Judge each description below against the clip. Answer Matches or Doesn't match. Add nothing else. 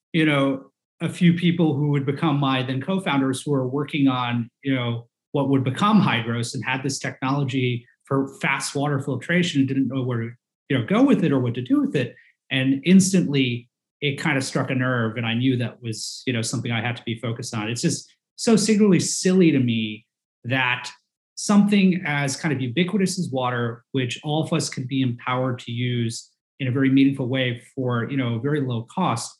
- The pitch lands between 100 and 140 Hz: Matches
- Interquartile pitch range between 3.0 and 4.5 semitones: Matches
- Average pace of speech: Doesn't match